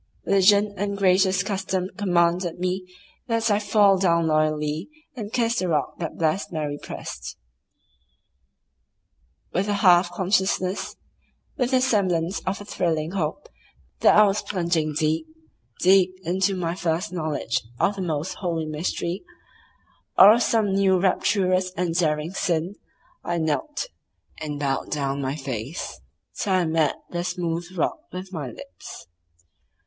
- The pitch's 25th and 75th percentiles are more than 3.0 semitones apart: Yes, average, 3.6 semitones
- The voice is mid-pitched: Yes, medium, 180 Hz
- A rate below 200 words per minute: Yes, average, 140 wpm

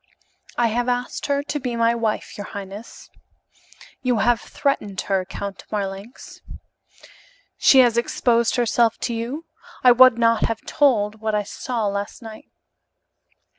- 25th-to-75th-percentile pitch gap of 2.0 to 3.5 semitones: Yes, average, 2.8 semitones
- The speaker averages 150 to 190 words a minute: No, average, 140 wpm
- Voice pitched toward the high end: Yes, high, 230 Hz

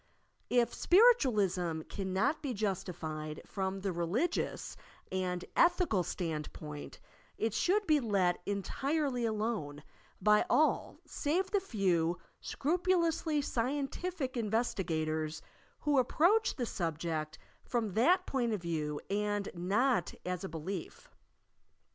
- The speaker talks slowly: Yes, slow, 110 wpm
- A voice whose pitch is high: Yes, high, 210 Hz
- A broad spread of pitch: Yes, wide, 8.2 semitones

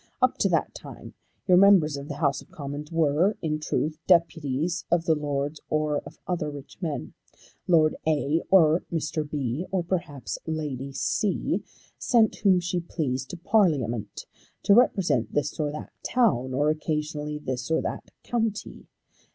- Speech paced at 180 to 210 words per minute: No, average, 155 wpm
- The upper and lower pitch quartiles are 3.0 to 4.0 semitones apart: Yes, average, 3.3 semitones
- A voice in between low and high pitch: Yes, medium, 155 Hz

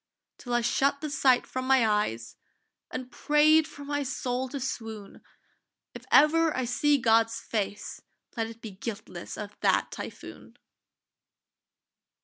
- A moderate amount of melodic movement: Yes, average, 4.2 semitones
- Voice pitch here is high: Yes, very high, 250 Hz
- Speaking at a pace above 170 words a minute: No, slow, 135 wpm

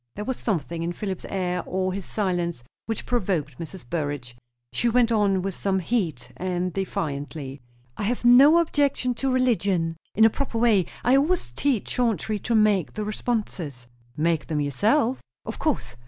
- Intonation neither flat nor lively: No, wide, 6.1 semitones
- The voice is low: No, high, 195 Hz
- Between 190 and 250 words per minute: No, average, 165 wpm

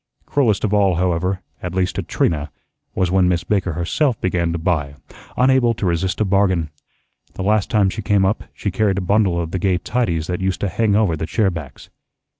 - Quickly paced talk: Yes, fast, 210 wpm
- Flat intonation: No, average, 3.2 semitones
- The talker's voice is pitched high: No, very low, 95 Hz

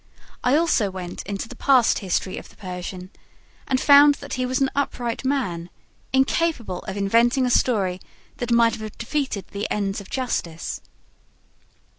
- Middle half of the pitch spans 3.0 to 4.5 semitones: No, wide, 5.4 semitones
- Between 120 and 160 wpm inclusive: Yes, average, 155 wpm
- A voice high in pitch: Yes, high, 230 Hz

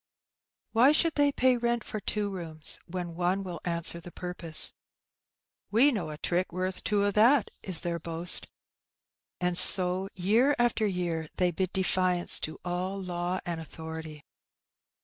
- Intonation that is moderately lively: Yes, average, 3.3 semitones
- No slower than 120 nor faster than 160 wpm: Yes, average, 150 wpm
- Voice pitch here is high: No, medium, 180 Hz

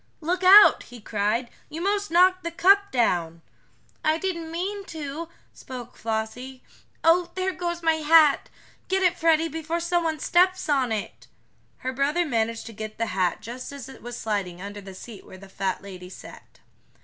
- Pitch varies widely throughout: Yes, wide, 7.7 semitones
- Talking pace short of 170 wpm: No, average, 175 wpm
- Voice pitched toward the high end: Yes, very high, 295 Hz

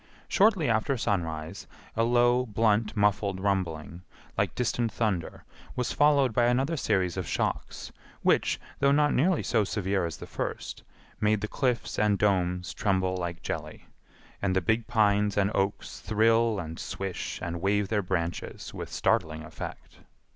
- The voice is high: No, low, 105 Hz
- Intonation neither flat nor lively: Yes, average, 3.9 semitones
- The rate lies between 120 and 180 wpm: Yes, average, 150 wpm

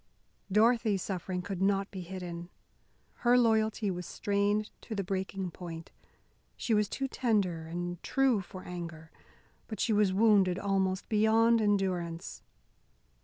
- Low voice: No, high, 195 Hz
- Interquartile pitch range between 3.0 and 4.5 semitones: Yes, average, 3.3 semitones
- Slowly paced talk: Yes, slow, 130 wpm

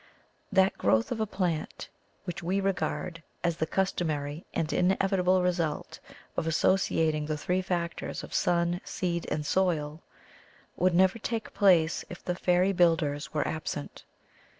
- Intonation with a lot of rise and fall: No, average, 2.9 semitones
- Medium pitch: Yes, medium, 175 Hz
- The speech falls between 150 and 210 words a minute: No, average, 140 wpm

